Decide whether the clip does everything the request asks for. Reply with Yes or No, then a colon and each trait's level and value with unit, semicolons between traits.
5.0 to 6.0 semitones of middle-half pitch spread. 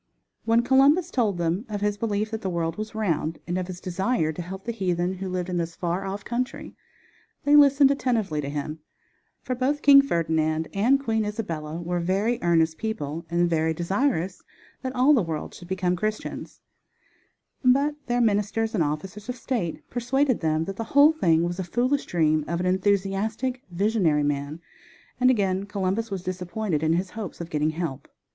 Yes: average, 5.3 semitones